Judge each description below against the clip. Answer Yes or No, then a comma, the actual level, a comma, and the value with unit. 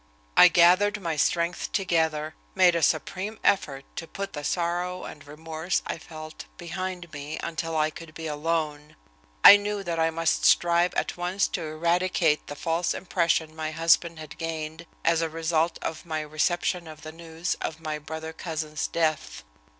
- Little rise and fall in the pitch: Yes, narrow, 1.8 semitones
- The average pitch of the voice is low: No, medium, 165 Hz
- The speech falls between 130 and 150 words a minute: No, average, 165 wpm